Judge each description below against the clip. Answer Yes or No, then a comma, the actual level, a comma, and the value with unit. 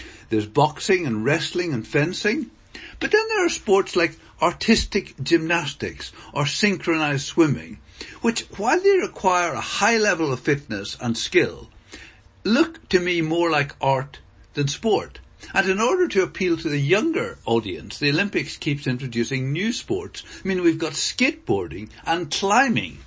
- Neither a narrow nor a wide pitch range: No, wide, 6.4 semitones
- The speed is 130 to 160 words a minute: Yes, average, 150 wpm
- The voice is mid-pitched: Yes, medium, 170 Hz